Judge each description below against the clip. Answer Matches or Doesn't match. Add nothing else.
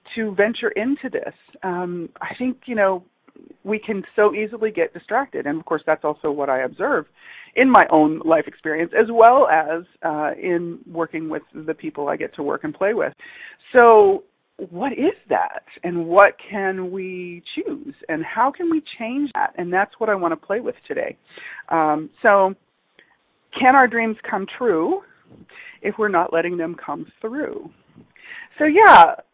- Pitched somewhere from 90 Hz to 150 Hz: Doesn't match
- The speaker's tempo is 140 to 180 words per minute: Matches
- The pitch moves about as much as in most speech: Doesn't match